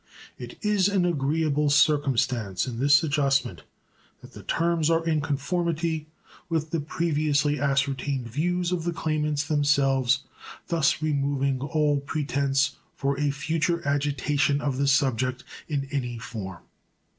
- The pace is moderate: No, slow, 130 wpm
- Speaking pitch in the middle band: Yes, medium, 145 Hz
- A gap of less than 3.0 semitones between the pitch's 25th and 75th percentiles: Yes, narrow, 2.5 semitones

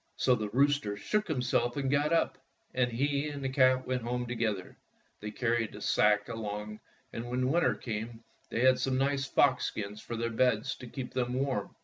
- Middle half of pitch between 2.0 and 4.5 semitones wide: Yes, average, 3.0 semitones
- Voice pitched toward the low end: Yes, low, 125 Hz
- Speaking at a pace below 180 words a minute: No, average, 195 wpm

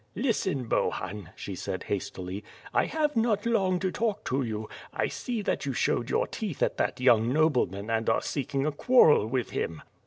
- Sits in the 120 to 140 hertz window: Yes, low, 135 Hz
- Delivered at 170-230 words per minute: Yes, average, 185 wpm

